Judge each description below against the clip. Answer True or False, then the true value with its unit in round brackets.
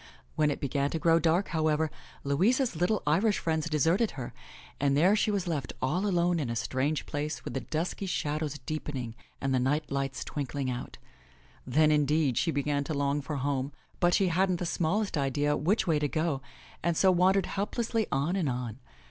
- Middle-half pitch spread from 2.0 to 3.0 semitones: False (4.0 semitones)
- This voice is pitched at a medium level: True (155 Hz)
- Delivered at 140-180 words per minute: False (190 wpm)